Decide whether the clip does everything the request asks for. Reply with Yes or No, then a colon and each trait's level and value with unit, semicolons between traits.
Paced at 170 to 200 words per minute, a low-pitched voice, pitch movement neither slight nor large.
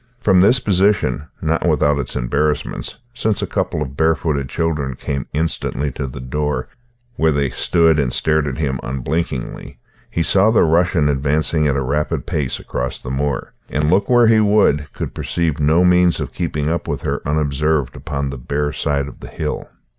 Yes: average, 180 wpm; very low, 75 Hz; average, 3.1 semitones